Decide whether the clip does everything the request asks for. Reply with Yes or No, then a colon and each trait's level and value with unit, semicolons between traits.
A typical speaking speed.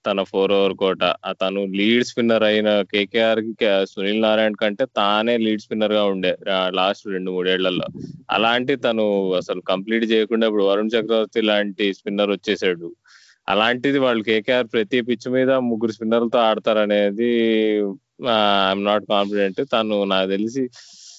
No: fast, 135 wpm